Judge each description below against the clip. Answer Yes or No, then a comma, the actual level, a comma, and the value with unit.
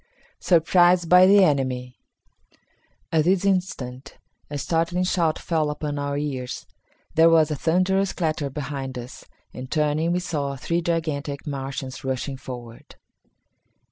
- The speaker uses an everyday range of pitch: Yes, average, 4.1 semitones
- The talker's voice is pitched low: No, medium, 150 Hz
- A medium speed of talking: No, slow, 130 wpm